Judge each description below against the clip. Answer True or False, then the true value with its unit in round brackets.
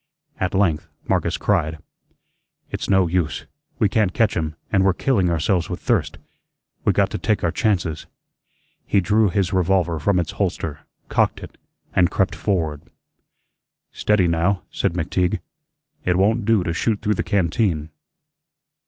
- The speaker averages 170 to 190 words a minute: False (150 wpm)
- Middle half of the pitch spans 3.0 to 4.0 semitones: True (3.4 semitones)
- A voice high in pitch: False (90 Hz)